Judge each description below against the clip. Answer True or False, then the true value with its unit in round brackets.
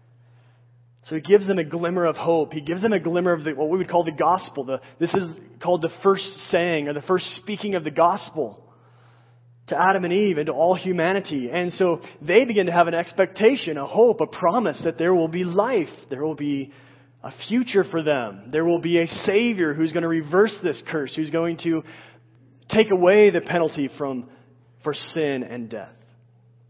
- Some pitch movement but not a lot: True (4.9 semitones)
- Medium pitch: True (165 Hz)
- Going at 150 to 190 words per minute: False (200 wpm)